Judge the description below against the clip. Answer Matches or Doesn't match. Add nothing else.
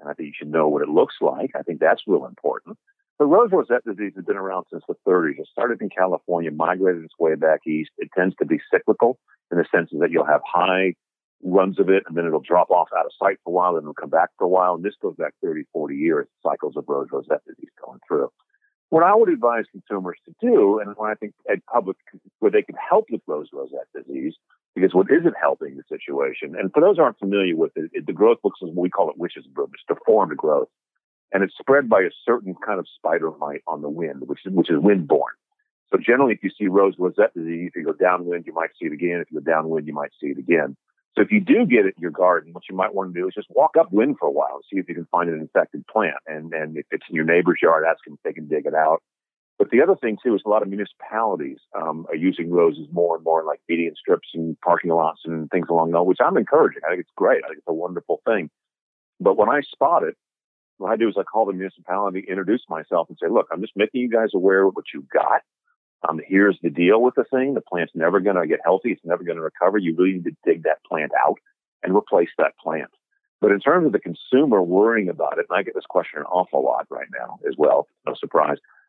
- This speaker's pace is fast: Matches